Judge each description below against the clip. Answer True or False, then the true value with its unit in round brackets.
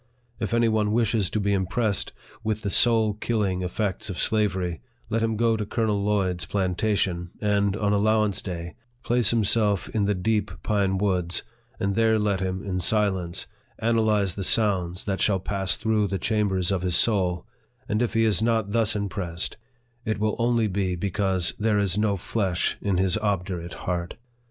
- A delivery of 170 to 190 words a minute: True (175 wpm)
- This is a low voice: True (100 Hz)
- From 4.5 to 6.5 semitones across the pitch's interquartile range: False (2.7 semitones)